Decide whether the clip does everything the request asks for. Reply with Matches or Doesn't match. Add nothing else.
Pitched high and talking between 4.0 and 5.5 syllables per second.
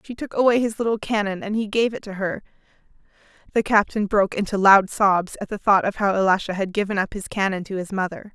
Doesn't match